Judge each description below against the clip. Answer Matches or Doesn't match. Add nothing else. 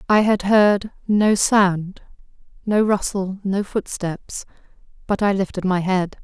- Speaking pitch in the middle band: Doesn't match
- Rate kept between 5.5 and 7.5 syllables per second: Doesn't match